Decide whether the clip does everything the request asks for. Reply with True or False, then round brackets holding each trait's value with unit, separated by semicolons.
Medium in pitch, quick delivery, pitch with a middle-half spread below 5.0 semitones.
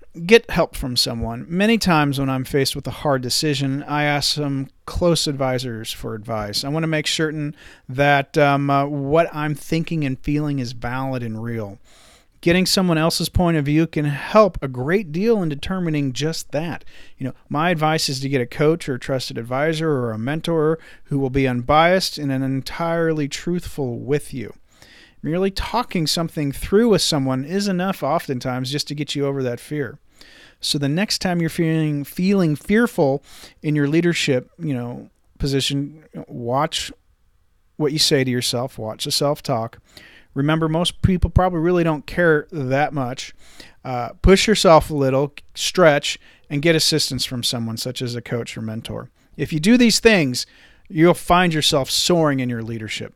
False (145 Hz; 175 wpm; 3.9 semitones)